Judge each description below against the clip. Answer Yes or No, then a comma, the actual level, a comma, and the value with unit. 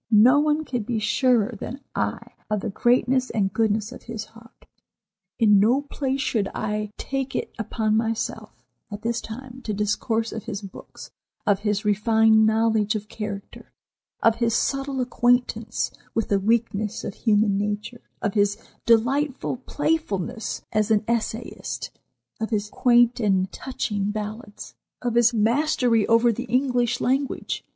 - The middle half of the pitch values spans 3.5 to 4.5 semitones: No, average, 2.7 semitones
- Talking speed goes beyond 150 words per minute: No, average, 145 wpm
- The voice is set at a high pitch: Yes, high, 225 Hz